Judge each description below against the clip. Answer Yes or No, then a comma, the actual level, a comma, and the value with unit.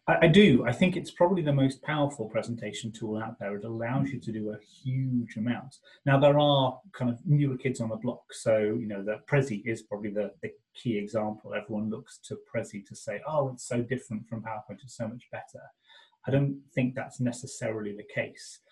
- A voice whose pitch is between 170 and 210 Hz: No, low, 120 Hz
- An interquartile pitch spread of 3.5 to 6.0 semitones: Yes, average, 3.9 semitones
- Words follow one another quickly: Yes, fast, 210 wpm